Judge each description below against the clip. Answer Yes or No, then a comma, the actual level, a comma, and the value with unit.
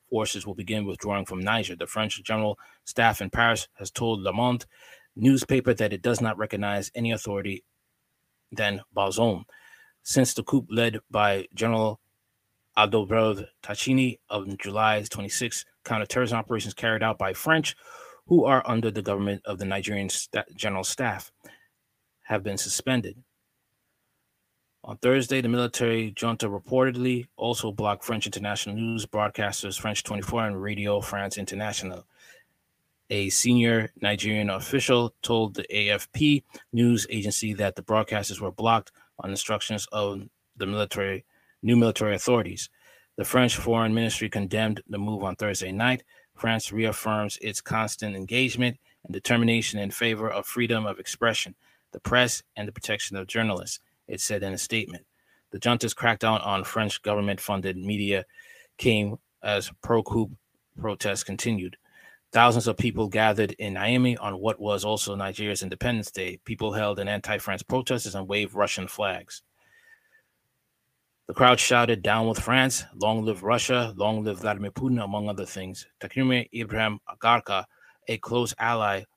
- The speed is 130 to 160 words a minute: Yes, average, 145 wpm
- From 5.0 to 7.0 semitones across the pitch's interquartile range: No, average, 2.7 semitones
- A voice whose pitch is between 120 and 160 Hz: No, low, 110 Hz